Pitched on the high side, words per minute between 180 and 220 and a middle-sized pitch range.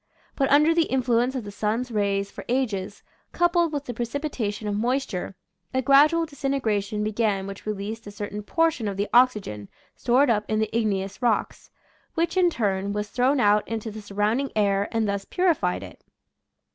Yes: high, 220 Hz; average, 185 wpm; average, 4.7 semitones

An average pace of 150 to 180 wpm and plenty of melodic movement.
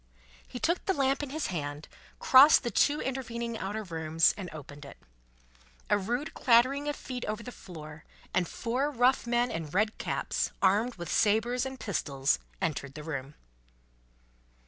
Yes: average, 160 wpm; wide, 8.1 semitones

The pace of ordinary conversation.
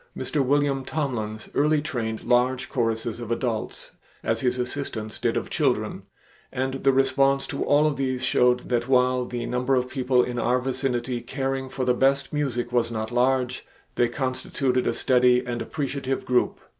Yes: average, 170 wpm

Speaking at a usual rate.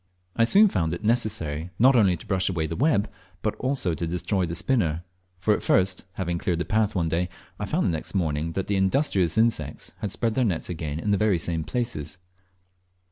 No: fast, 210 wpm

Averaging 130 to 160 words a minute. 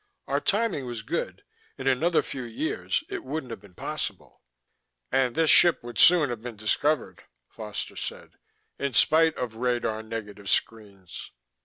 Yes: average, 150 wpm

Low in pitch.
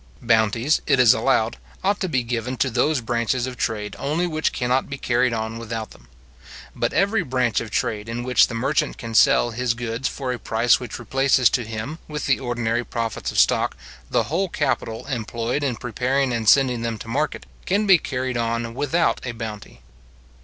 Yes: low, 120 Hz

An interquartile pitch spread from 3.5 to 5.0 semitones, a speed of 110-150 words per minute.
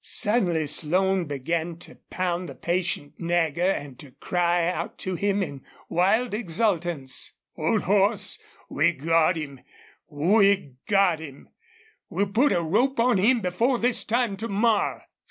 Yes: average, 4.1 semitones; average, 140 wpm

